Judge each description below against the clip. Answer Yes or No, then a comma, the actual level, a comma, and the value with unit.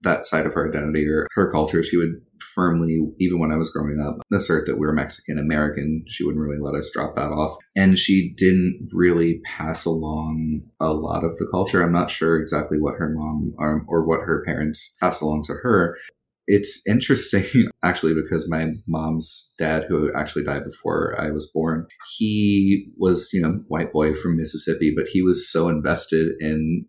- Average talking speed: Yes, average, 190 wpm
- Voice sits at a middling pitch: No, very low, 80 Hz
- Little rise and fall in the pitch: Yes, narrow, 2.3 semitones